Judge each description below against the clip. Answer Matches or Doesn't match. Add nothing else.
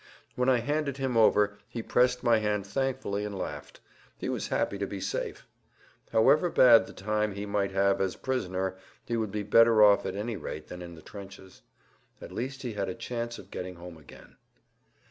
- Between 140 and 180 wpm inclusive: Doesn't match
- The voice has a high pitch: Doesn't match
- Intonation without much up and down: Doesn't match